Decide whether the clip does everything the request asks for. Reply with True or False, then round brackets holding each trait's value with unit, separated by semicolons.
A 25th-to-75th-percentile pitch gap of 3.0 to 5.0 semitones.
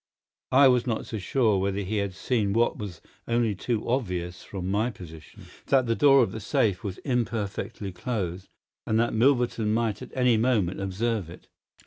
True (3.7 semitones)